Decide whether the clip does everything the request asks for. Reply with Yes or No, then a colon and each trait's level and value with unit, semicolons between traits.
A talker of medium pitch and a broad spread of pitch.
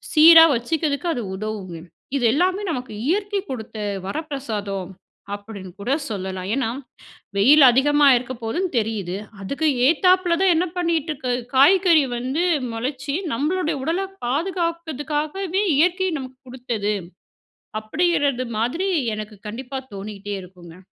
No: very high, 275 Hz; wide, 7.4 semitones